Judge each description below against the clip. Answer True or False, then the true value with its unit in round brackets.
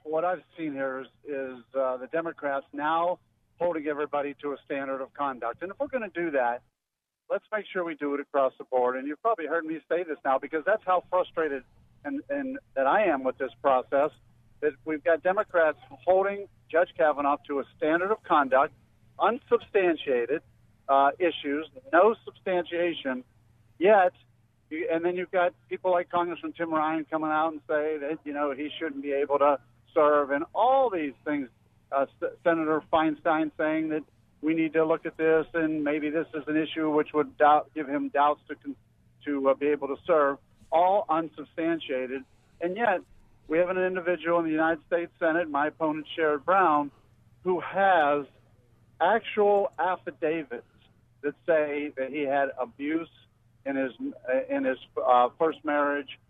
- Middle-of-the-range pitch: True (150 Hz)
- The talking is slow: False (175 wpm)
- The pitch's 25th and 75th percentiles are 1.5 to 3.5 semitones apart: False (3.9 semitones)